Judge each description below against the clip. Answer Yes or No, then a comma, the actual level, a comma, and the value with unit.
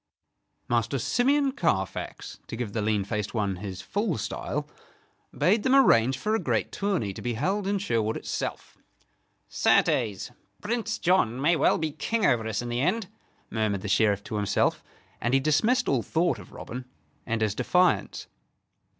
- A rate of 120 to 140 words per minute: No, average, 165 wpm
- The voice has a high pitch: No, low, 125 Hz